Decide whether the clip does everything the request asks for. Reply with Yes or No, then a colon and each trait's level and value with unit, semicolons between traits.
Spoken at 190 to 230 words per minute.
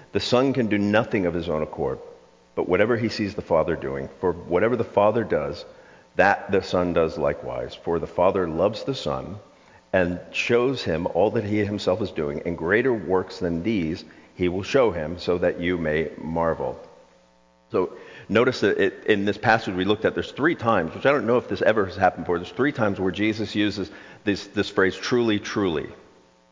Yes: average, 200 wpm